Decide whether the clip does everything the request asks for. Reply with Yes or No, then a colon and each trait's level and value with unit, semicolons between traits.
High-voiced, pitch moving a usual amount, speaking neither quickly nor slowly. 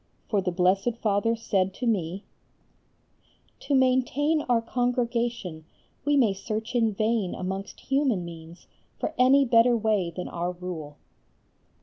No: high, 220 Hz; average, 5.0 semitones; slow, 130 wpm